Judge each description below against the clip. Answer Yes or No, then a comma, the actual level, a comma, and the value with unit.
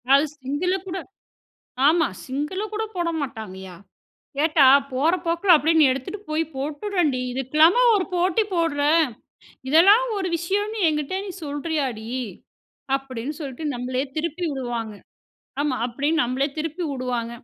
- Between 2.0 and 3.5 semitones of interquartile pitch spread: No, average, 4.6 semitones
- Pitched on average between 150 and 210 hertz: No, very high, 300 Hz